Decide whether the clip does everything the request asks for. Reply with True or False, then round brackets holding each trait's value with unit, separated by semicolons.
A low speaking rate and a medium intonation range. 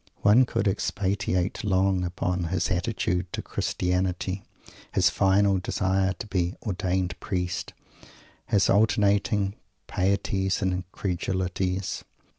False (105 wpm; 1.6 semitones)